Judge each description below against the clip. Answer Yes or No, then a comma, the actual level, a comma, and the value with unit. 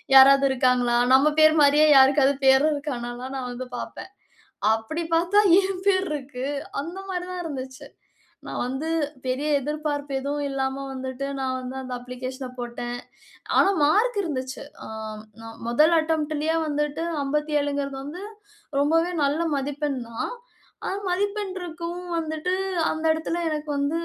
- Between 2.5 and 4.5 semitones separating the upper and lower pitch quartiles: Yes, average, 3.3 semitones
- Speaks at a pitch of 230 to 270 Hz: No, very high, 290 Hz